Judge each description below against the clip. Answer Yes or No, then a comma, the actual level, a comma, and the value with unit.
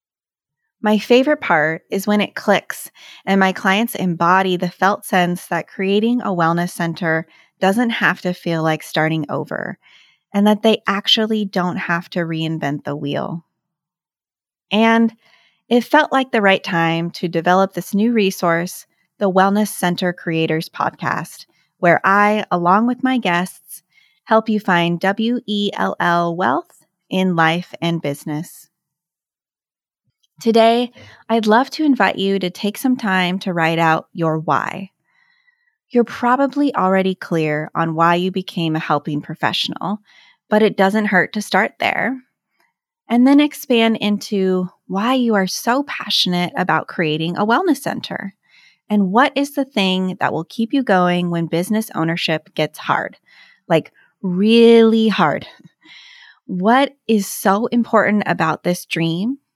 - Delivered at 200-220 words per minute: No, average, 140 wpm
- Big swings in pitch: No, average, 4.8 semitones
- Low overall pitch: No, high, 190 Hz